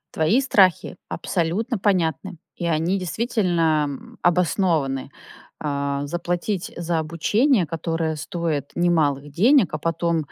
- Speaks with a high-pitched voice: No, medium, 170 Hz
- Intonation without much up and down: No, average, 3.1 semitones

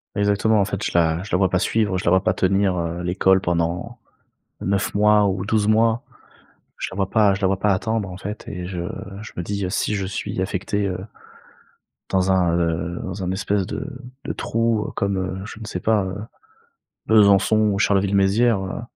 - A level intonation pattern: Yes, narrow, 2.2 semitones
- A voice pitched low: Yes, very low, 95 Hz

